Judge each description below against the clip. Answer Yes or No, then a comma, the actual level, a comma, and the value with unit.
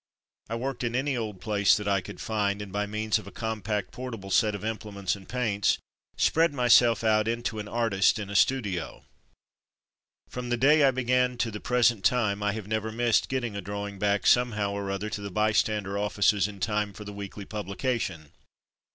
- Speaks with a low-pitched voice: Yes, low, 105 Hz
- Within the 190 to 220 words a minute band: Yes, average, 195 wpm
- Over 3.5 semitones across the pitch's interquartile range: No, average, 2.8 semitones